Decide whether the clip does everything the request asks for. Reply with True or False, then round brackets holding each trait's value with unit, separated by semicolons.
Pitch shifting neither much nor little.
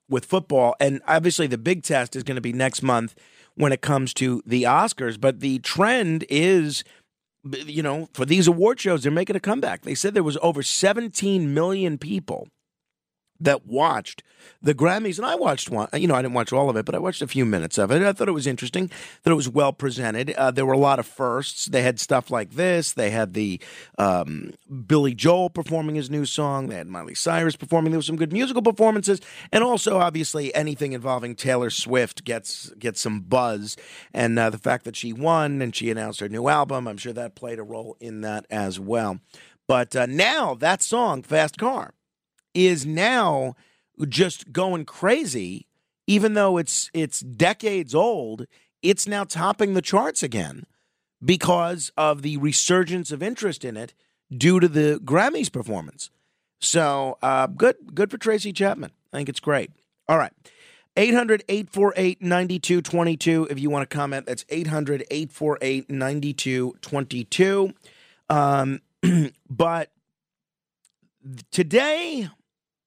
False (5.9 semitones)